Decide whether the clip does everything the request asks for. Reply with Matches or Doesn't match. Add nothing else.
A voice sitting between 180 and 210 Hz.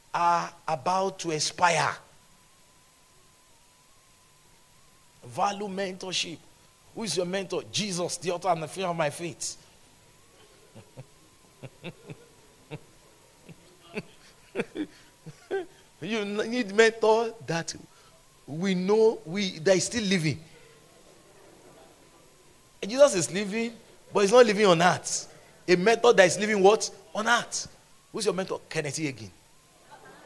Matches